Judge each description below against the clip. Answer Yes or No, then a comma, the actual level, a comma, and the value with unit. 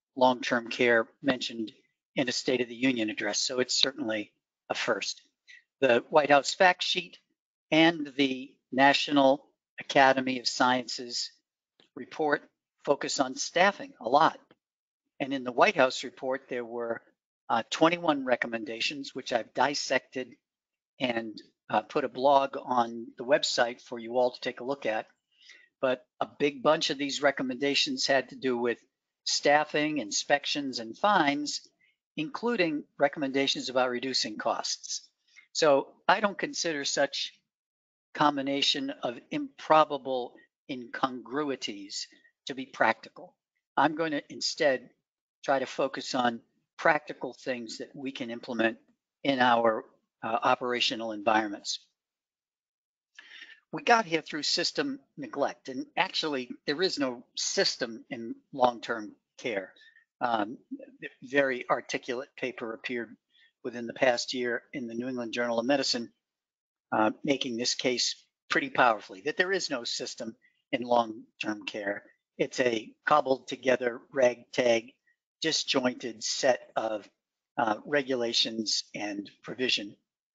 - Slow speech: Yes, slow, 130 wpm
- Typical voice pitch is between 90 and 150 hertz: Yes, low, 135 Hz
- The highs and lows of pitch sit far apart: Yes, wide, 5.9 semitones